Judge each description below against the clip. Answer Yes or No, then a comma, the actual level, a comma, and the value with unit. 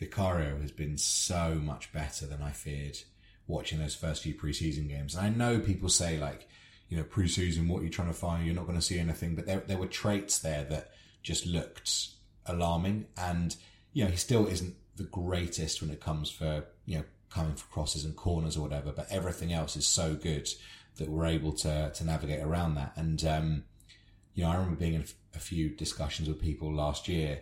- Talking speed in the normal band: No, fast, 210 wpm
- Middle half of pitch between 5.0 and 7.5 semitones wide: No, average, 3.2 semitones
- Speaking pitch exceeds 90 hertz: No, very low, 85 Hz